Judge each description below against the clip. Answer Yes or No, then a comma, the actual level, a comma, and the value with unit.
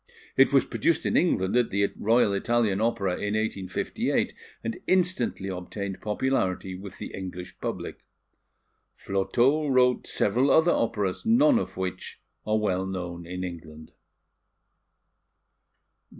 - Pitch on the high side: No, low, 100 Hz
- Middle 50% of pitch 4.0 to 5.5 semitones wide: Yes, average, 4.6 semitones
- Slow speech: Yes, slow, 120 wpm